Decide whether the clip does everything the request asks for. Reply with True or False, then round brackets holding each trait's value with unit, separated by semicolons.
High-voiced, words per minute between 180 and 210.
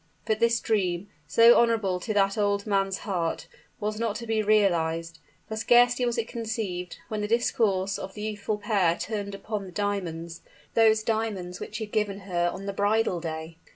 True (205 Hz; 185 wpm)